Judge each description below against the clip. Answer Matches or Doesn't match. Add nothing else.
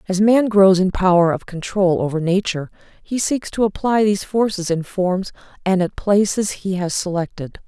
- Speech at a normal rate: Matches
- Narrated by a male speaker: Doesn't match